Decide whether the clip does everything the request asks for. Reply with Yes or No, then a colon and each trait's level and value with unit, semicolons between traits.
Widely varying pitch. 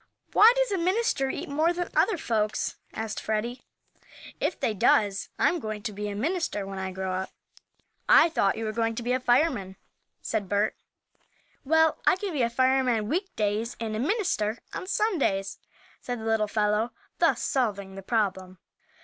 Yes: wide, 7.0 semitones